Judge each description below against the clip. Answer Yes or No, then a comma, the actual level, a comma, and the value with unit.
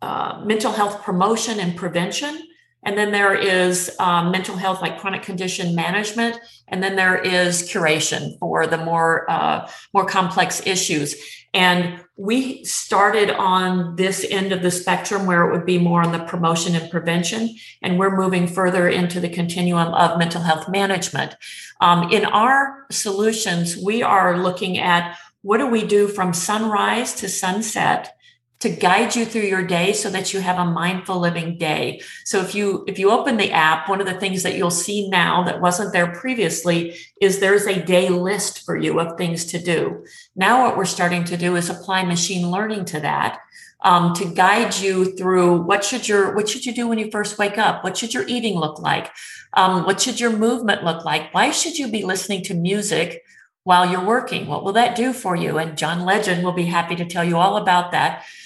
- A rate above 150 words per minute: Yes, average, 195 wpm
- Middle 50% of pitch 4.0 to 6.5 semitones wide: No, average, 2.7 semitones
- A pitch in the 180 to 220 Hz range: Yes, medium, 185 Hz